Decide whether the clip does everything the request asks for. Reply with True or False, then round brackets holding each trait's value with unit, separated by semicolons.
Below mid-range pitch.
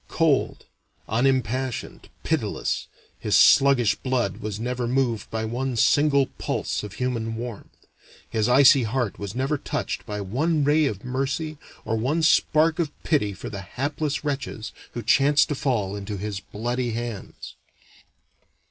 True (125 Hz)